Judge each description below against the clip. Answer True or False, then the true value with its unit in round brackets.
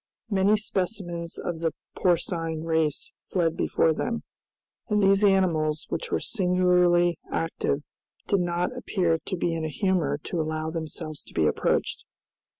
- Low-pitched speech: False (175 Hz)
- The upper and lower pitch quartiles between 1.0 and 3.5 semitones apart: True (2.8 semitones)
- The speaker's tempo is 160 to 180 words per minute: False (145 wpm)